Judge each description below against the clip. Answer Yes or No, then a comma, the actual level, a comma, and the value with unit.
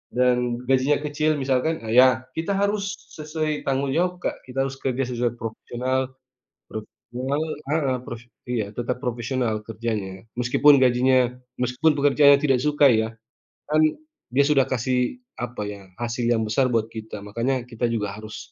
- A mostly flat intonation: No, average, 3.2 semitones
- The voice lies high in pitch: No, low, 130 Hz